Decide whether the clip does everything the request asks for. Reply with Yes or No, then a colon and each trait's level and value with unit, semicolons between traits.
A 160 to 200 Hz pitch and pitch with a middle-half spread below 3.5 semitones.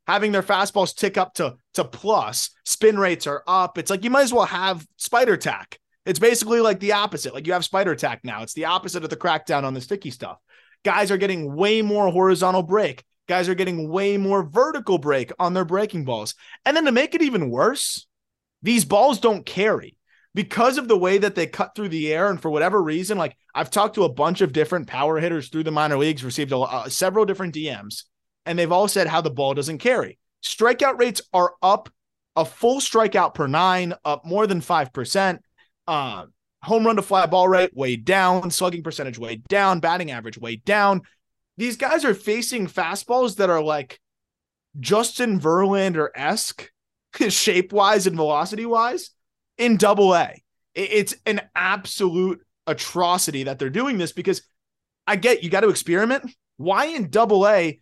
No: medium, 185 Hz; average, 4.8 semitones